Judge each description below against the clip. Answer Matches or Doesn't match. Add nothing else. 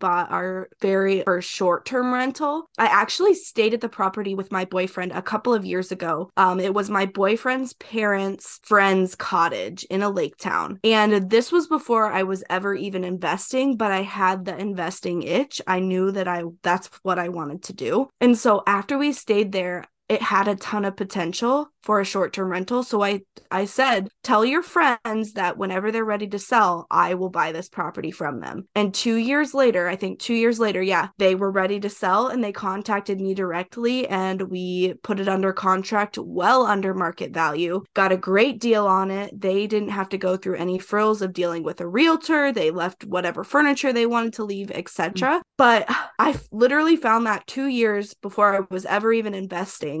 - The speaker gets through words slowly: Doesn't match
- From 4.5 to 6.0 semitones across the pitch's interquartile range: Doesn't match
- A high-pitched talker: Matches